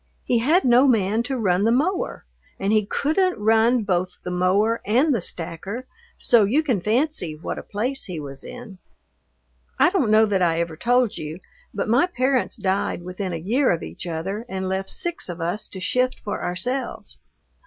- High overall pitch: Yes, high, 215 Hz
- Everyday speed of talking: Yes, average, 185 wpm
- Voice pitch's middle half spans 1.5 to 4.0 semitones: No, wide, 5.6 semitones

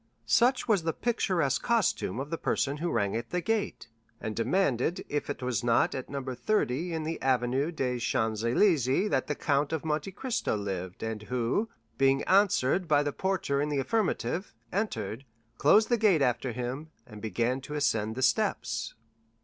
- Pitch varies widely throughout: Yes, wide, 6.6 semitones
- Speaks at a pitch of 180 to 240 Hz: No, medium, 140 Hz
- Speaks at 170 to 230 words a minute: Yes, average, 175 wpm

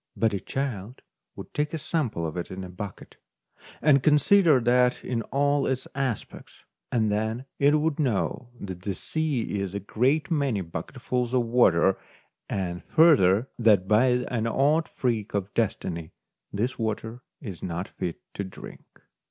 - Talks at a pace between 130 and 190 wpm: Yes, average, 155 wpm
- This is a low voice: Yes, low, 115 Hz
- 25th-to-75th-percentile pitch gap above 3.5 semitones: Yes, wide, 5.6 semitones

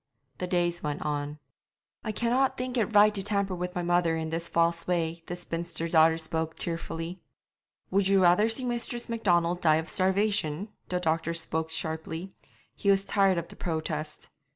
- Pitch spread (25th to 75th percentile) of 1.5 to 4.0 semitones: Yes, average, 3.4 semitones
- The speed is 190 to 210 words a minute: No, average, 175 wpm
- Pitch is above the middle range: No, medium, 175 Hz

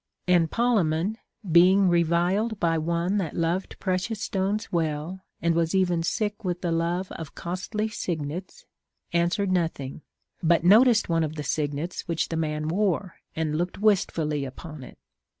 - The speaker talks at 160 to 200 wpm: No, average, 150 wpm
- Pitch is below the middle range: No, medium, 170 Hz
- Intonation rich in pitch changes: No, average, 3.0 semitones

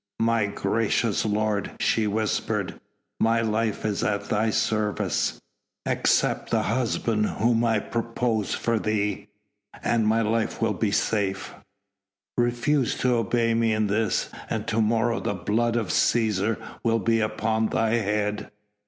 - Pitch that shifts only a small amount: Yes, narrow, 1.5 semitones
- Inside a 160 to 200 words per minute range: No, slow, 135 wpm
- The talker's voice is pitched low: Yes, low, 110 Hz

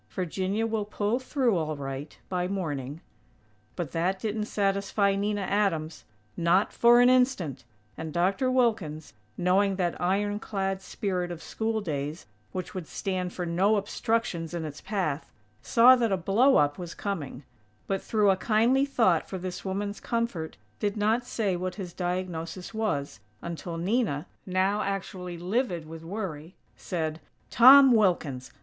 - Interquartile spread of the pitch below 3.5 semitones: No, average, 4.0 semitones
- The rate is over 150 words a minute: No, average, 145 wpm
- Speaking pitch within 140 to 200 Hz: Yes, high, 190 Hz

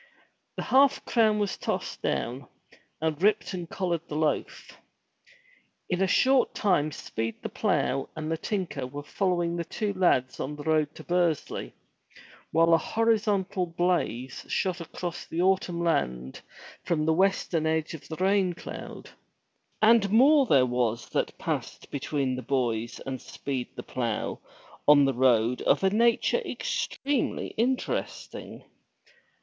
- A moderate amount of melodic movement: No, wide, 6.0 semitones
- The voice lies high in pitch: No, medium, 165 Hz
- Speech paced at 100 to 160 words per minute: Yes, average, 145 wpm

